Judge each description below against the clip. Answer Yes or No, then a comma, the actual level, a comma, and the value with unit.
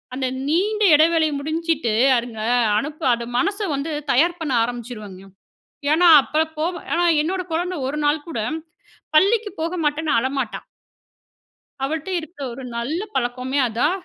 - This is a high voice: Yes, very high, 305 Hz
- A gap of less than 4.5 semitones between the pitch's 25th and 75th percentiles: No, average, 4.8 semitones